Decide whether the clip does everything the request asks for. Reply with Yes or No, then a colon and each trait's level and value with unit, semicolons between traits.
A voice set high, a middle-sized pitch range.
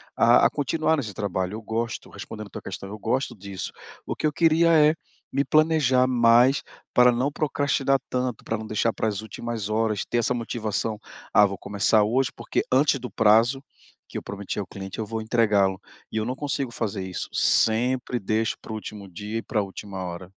No: low, 115 Hz; average, 3.7 semitones